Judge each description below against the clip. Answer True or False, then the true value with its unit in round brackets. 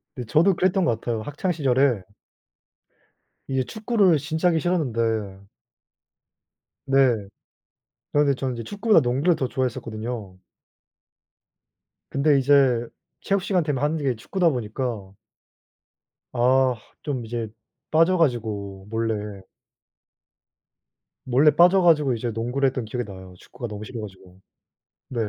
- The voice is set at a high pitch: False (130 Hz)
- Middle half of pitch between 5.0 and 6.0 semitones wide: True (5.4 semitones)